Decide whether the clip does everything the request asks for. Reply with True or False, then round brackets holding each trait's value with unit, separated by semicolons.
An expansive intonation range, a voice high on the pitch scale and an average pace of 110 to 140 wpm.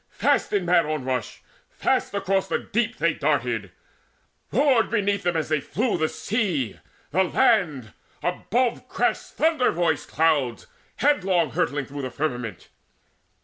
False (6.3 semitones; 170 Hz; 135 wpm)